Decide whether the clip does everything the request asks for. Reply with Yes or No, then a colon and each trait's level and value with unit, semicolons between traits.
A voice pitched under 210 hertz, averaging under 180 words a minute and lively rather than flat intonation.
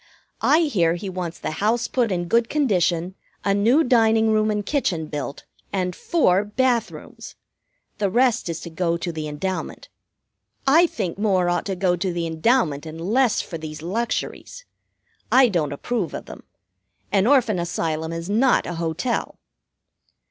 Yes: high, 190 Hz; average, 165 wpm; wide, 5.7 semitones